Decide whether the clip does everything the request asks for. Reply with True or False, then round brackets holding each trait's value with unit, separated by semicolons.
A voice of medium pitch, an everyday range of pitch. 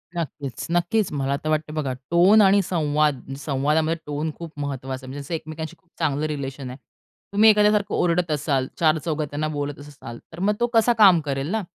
True (155 Hz; 3.5 semitones)